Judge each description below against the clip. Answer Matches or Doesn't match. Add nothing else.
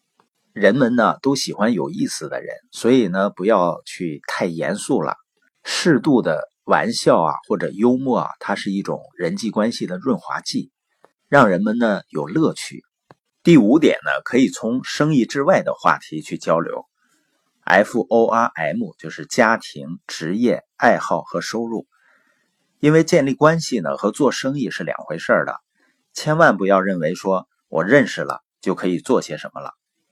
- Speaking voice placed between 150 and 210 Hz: Doesn't match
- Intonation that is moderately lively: Doesn't match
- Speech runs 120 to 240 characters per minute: Matches